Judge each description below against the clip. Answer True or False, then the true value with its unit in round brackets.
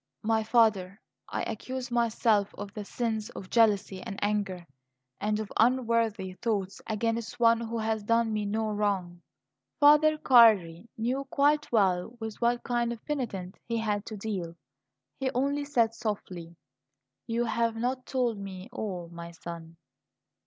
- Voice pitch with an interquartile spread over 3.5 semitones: False (3.1 semitones)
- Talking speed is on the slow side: False (145 wpm)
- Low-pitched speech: False (220 Hz)